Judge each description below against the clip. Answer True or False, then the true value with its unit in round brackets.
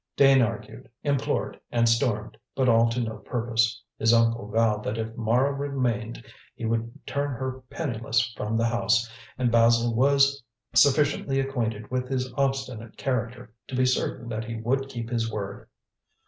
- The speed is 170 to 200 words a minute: False (160 wpm)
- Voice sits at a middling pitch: False (120 Hz)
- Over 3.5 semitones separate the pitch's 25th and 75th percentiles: False (2.5 semitones)